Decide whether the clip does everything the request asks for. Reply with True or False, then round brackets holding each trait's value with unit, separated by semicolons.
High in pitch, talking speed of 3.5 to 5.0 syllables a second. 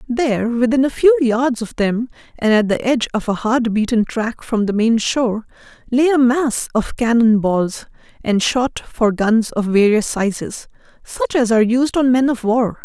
True (235 Hz; 4.5 syllables/s)